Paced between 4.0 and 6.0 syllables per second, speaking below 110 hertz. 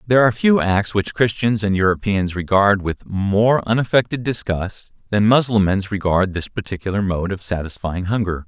Yes: 5.1 syllables/s; low, 100 Hz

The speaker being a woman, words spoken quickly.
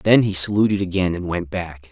No: male; fast, 220 wpm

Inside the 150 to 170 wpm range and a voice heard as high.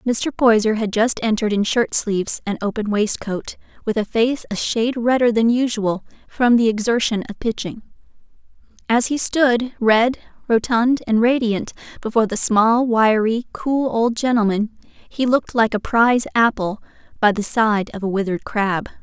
Yes: average, 160 wpm; high, 225 Hz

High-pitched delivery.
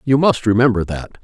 No: low, 115 Hz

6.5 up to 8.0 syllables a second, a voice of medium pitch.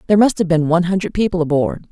Yes: 7.6 syllables/s; medium, 180 Hz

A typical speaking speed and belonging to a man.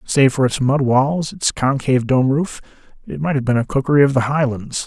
No: fast, 220 wpm; male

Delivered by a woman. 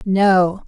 Yes: female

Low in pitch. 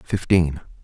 Yes: very low, 85 Hz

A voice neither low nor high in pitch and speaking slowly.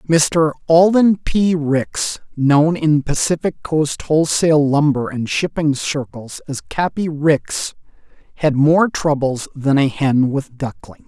Yes: medium, 150 Hz; slow, 130 wpm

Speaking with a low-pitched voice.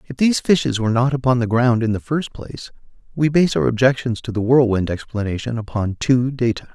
Yes: low, 120 Hz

